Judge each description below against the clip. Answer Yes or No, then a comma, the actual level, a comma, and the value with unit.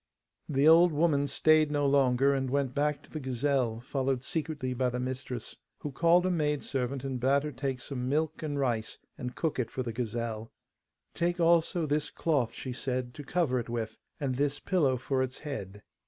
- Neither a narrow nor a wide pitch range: Yes, average, 3.1 semitones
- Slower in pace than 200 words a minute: Yes, average, 190 wpm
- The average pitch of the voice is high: No, low, 135 Hz